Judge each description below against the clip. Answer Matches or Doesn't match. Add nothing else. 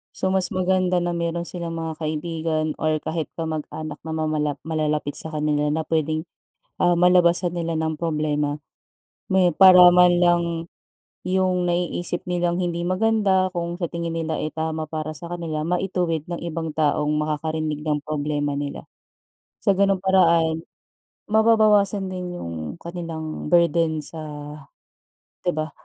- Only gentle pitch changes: Matches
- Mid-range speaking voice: Matches